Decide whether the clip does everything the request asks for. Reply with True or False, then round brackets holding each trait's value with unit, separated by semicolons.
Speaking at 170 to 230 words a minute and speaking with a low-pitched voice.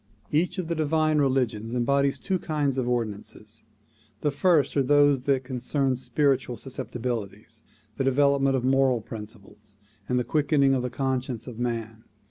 False (155 wpm; 130 Hz)